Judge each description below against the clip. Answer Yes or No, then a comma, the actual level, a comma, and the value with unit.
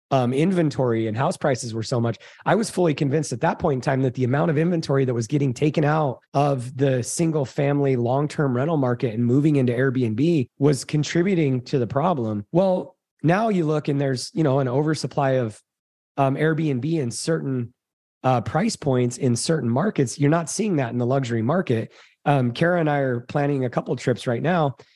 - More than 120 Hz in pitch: Yes, medium, 140 Hz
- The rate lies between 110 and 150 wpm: No, average, 200 wpm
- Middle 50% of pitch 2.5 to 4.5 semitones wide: Yes, average, 3.7 semitones